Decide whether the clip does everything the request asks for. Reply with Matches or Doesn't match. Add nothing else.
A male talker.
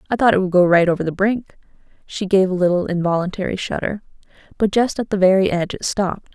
Doesn't match